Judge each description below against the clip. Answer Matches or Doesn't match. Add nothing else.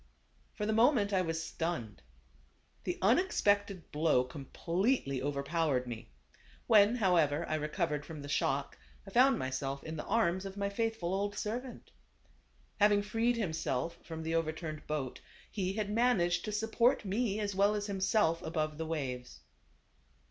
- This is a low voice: Doesn't match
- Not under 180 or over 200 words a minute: Doesn't match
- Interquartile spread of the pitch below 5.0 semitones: Doesn't match